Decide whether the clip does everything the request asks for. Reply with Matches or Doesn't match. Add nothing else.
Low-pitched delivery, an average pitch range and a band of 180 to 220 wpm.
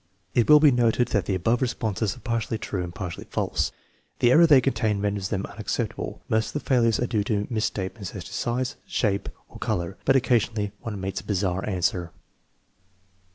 Matches